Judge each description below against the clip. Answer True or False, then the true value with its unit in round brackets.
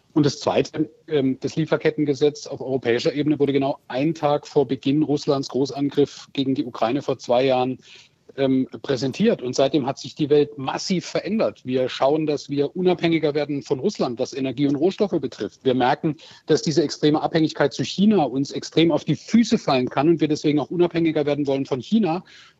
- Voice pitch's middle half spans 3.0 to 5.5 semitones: False (2.4 semitones)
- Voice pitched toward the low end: False (145 Hz)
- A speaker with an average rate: True (180 wpm)